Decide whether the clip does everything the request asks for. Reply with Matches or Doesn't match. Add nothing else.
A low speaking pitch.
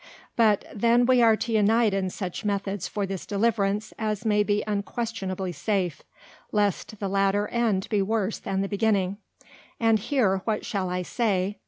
Doesn't match